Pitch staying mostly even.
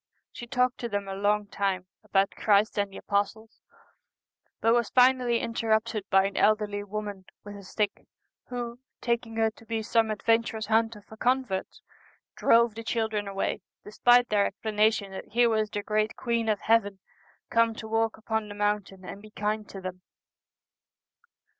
Yes: narrow, 2.1 semitones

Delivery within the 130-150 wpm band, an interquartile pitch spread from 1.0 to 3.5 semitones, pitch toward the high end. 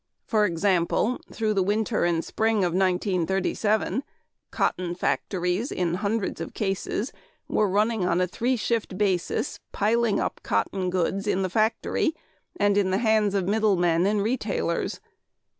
Yes: average, 145 wpm; average, 3.0 semitones; high, 200 Hz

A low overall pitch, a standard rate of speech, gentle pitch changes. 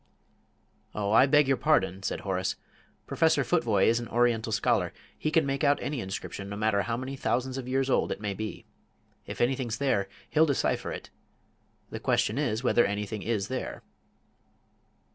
No: low, 120 Hz; average, 170 wpm; average, 4.6 semitones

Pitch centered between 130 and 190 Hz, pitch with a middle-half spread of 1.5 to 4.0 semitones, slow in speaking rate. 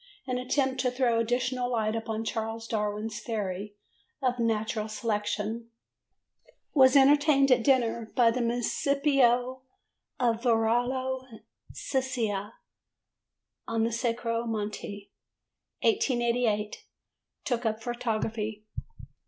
No: high, 235 Hz; narrow, 2.4 semitones; slow, 95 wpm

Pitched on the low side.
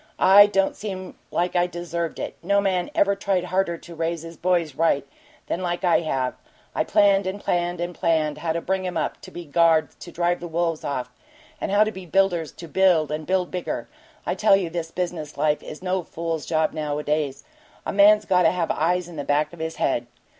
No: medium, 175 Hz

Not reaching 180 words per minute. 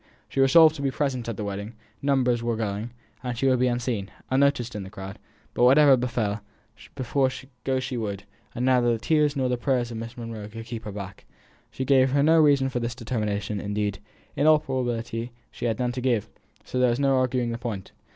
No: fast, 205 wpm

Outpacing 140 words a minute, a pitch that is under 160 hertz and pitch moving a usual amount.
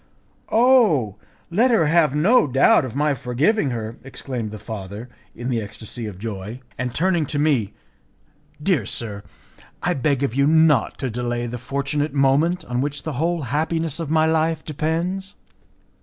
Yes: average, 160 wpm; medium, 140 Hz; average, 5.0 semitones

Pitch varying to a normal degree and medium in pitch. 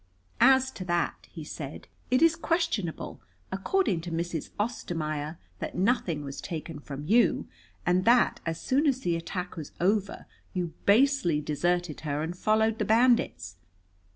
No: wide, 6.5 semitones; medium, 180 Hz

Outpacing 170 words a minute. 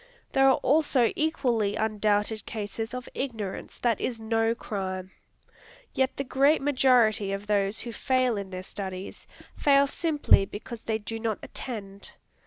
No: average, 145 wpm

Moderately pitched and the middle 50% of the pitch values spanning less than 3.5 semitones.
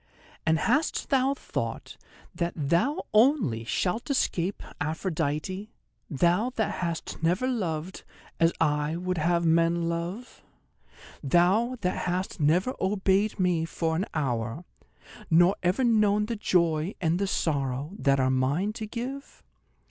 No: medium, 175 Hz; average, 4.6 semitones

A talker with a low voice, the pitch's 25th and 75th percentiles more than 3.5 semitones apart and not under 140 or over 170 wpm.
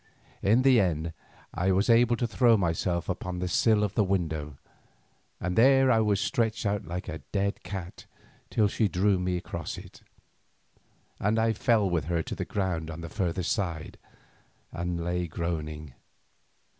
Yes: very low, 95 Hz; average, 4.2 semitones; average, 165 wpm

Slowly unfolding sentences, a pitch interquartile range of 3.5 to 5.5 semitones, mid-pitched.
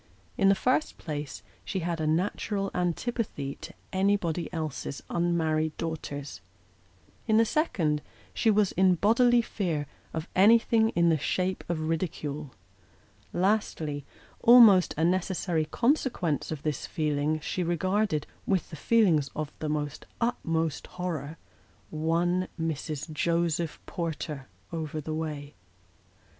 Yes: slow, 120 wpm; average, 4.0 semitones; medium, 170 Hz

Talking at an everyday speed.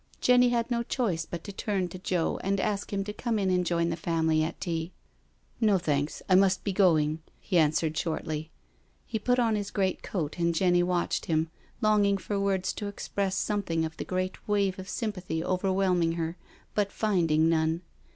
Yes: average, 190 wpm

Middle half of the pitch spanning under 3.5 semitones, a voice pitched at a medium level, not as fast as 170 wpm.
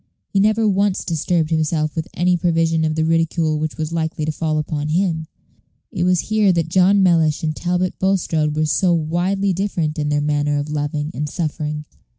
No: average, 2.9 semitones; medium, 160 Hz; average, 185 wpm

